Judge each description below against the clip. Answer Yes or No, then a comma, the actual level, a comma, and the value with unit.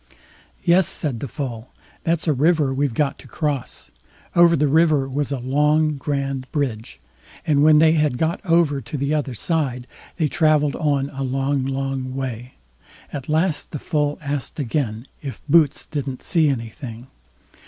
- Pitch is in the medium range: Yes, medium, 145 Hz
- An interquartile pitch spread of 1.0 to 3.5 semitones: Yes, narrow, 2.6 semitones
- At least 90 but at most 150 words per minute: No, average, 160 wpm